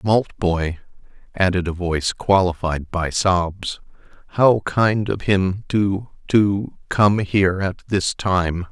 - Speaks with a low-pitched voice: Yes, very low, 95 Hz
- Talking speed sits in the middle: No, slow, 110 wpm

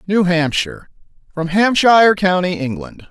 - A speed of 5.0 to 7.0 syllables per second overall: No, 4.8 syllables/s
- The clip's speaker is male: Yes, male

